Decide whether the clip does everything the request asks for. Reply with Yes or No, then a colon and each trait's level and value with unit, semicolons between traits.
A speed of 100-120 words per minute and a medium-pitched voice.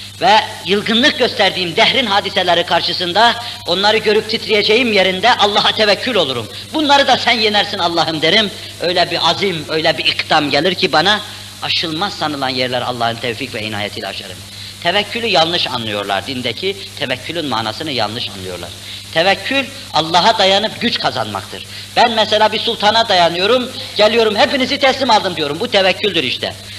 No: fast, 140 wpm; medium, 175 Hz